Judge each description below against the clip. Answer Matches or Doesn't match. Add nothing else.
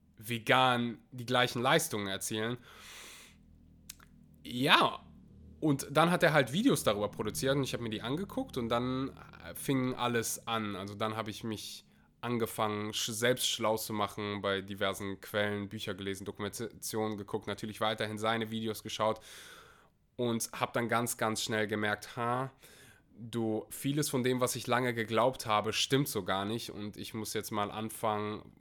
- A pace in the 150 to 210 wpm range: Matches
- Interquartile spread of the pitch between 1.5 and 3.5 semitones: Matches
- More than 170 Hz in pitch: Doesn't match